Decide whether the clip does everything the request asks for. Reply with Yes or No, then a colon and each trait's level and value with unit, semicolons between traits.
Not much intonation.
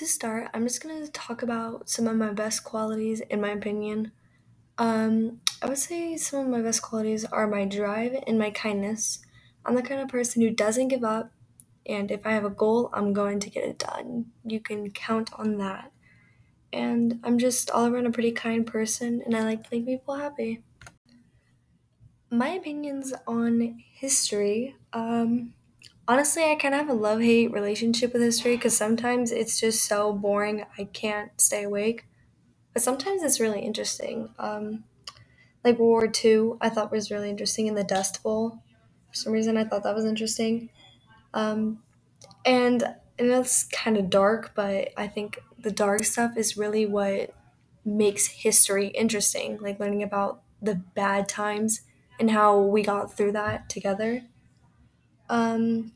Yes: narrow, 2.2 semitones